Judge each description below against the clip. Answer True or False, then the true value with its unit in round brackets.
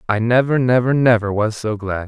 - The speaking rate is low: False (200 wpm)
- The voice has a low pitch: True (115 Hz)